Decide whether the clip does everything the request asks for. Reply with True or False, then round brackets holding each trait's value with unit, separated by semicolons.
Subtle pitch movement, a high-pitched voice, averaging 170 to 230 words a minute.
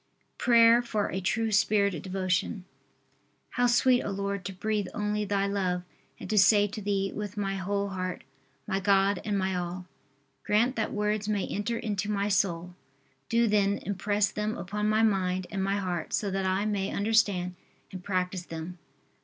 True (2.0 semitones; 200 Hz; 175 wpm)